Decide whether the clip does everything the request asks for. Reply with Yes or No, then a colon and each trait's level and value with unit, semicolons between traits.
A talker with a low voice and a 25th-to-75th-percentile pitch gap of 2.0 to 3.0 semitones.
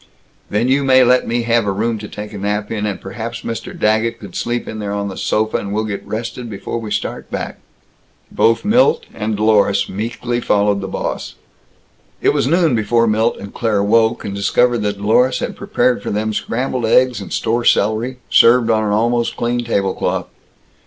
Yes: low, 110 Hz; narrow, 2.5 semitones